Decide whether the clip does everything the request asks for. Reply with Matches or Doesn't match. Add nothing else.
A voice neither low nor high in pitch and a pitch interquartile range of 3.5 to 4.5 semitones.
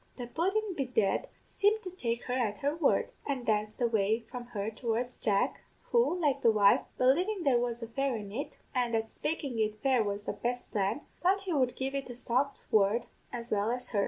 Doesn't match